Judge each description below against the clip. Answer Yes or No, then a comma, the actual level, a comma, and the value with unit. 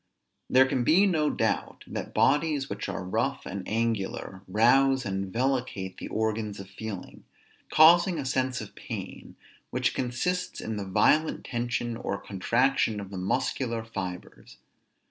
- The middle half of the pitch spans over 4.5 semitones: Yes, average, 5.1 semitones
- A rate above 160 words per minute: No, average, 145 wpm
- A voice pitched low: Yes, low, 115 Hz